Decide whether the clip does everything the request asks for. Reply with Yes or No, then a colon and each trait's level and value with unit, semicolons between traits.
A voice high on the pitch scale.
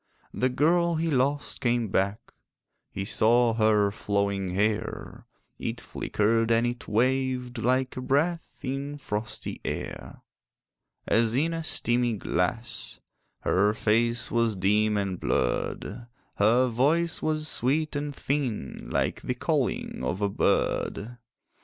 No: low, 120 Hz